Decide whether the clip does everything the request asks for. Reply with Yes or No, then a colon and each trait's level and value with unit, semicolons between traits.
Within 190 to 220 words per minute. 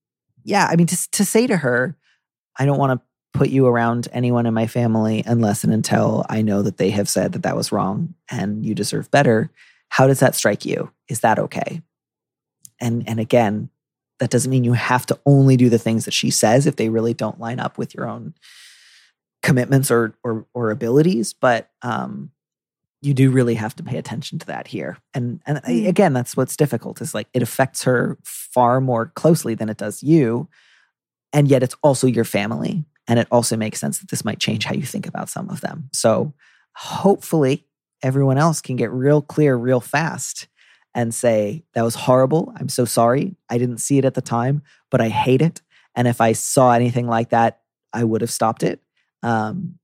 Yes: average, 200 wpm